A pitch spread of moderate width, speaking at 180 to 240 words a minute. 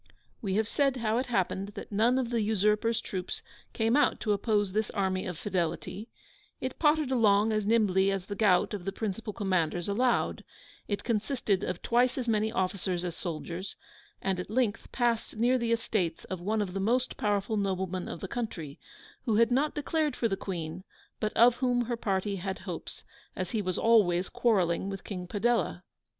Yes: average, 3.6 semitones; average, 185 wpm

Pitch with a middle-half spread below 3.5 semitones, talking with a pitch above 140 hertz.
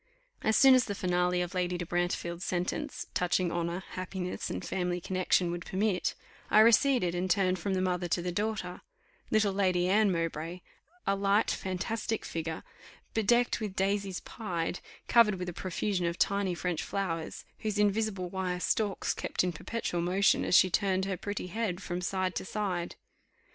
Yes: narrow, 2.4 semitones; medium, 185 Hz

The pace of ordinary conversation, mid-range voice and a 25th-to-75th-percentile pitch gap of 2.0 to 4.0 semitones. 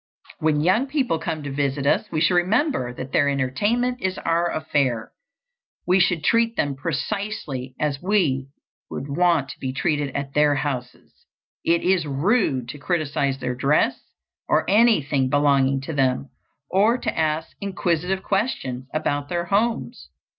No: average, 150 wpm; medium, 150 Hz; average, 5.3 semitones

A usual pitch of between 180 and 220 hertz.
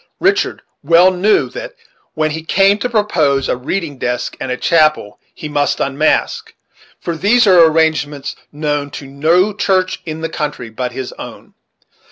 No: medium, 160 Hz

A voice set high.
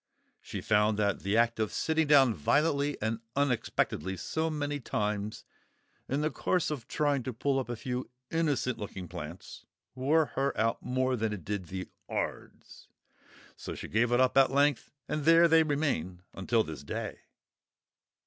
No: low, 125 Hz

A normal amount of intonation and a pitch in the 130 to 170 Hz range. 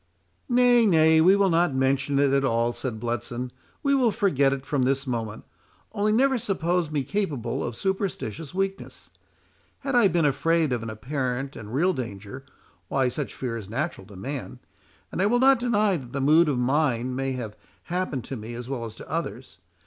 No: wide, 7.0 semitones; medium, 140 Hz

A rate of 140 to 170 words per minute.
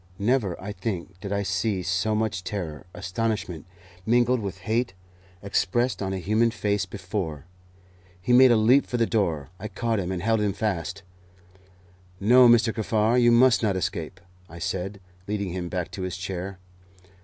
Yes: average, 165 wpm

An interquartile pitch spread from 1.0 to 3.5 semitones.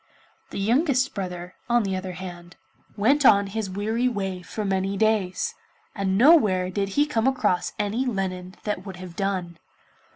Yes: average, 3.2 semitones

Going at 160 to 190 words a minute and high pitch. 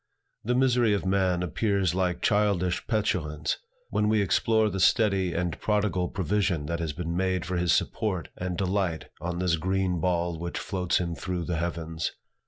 No: average, 170 wpm; very low, 90 Hz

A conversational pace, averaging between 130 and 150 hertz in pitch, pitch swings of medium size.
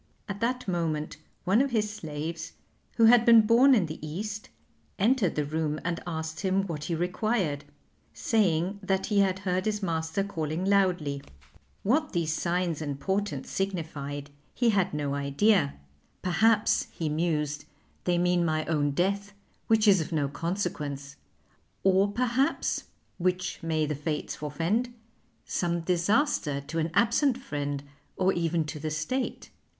No: average, 145 wpm; medium, 175 Hz; average, 4.7 semitones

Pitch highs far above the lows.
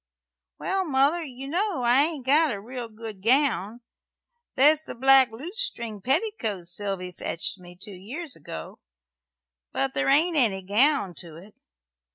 Yes: wide, 6.9 semitones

